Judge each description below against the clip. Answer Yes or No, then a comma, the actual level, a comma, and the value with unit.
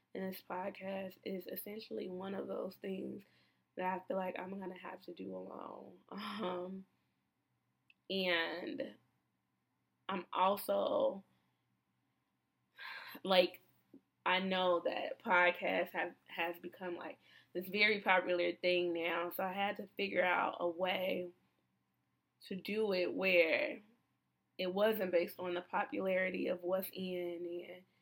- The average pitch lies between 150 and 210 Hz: Yes, medium, 185 Hz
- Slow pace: Yes, slow, 125 wpm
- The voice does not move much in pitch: Yes, narrow, 1.6 semitones